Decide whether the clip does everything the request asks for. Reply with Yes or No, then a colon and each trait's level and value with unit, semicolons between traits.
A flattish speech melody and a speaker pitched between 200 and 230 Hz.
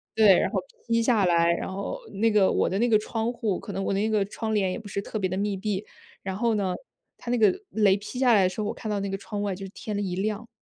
Yes: narrow, 2.2 semitones; high, 205 Hz